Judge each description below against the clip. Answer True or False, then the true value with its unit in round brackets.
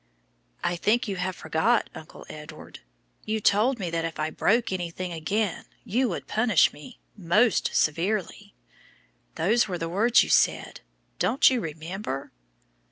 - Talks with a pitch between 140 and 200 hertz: True (185 Hz)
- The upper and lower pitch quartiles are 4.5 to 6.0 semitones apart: True (4.9 semitones)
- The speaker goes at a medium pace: True (145 wpm)